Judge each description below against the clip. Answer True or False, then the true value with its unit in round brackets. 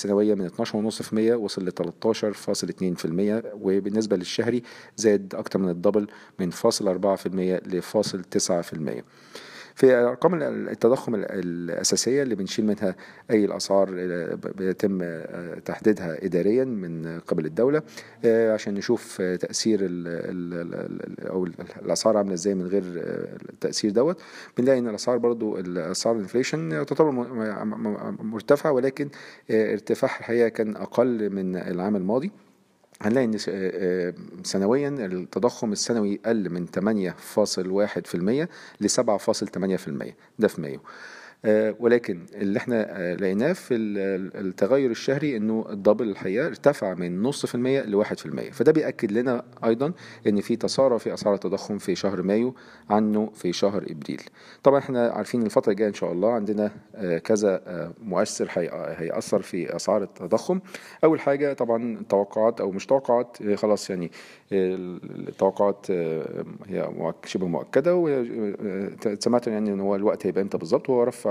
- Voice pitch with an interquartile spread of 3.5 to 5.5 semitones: True (3.9 semitones)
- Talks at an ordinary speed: True (120 wpm)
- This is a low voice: True (105 Hz)